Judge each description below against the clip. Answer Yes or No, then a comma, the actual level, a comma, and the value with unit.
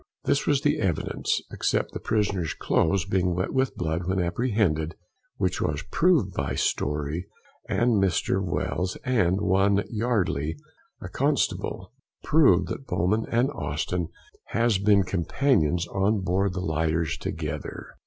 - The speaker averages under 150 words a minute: Yes, slow, 135 wpm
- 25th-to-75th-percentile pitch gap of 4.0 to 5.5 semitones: Yes, average, 4.4 semitones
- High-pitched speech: No, very low, 95 Hz